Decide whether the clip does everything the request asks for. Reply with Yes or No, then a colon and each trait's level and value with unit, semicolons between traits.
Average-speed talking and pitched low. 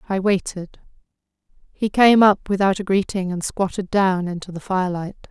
No: average, 160 wpm; high, 190 Hz